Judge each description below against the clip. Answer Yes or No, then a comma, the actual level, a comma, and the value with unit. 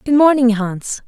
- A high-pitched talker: Yes, high, 245 Hz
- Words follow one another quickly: No, average, 165 wpm